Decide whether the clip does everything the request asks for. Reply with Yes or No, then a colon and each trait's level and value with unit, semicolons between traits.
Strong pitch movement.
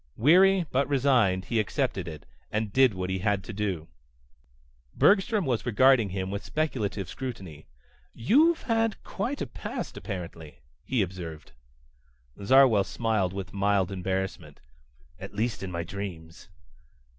Yes: wide, 6.1 semitones